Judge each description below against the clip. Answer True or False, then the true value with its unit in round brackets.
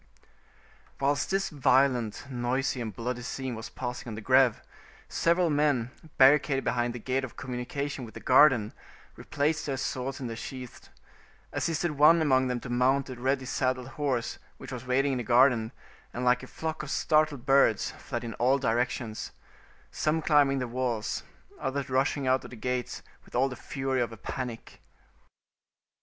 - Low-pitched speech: True (130 Hz)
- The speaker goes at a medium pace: True (170 wpm)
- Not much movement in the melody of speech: True (2.3 semitones)